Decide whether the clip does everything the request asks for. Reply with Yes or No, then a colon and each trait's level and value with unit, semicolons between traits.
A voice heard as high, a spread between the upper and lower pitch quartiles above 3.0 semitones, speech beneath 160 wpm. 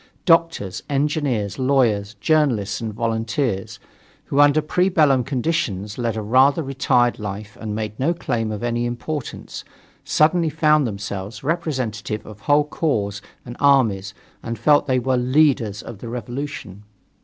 No: low, 120 Hz; average, 5.3 semitones; average, 145 wpm